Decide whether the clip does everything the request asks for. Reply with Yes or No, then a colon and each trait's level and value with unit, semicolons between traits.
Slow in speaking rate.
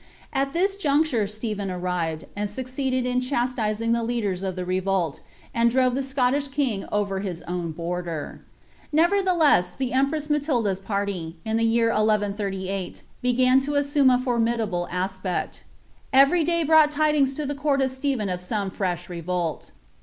No: average, 160 wpm